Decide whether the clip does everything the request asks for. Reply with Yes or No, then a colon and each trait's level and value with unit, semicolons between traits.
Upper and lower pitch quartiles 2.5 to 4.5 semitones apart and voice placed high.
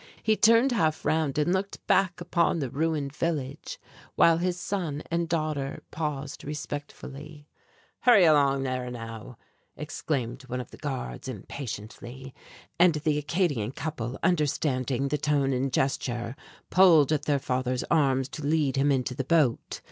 No: average, 3.7 semitones; medium, 145 Hz